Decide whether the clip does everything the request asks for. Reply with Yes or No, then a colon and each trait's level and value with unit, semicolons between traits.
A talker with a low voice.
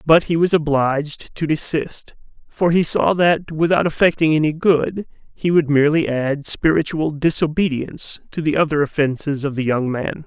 No: medium, 155 Hz